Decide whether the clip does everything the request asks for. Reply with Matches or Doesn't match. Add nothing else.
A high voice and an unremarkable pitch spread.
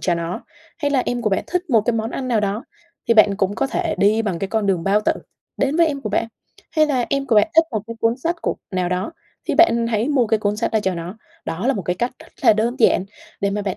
Matches